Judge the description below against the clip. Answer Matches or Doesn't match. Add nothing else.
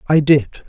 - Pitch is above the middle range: Doesn't match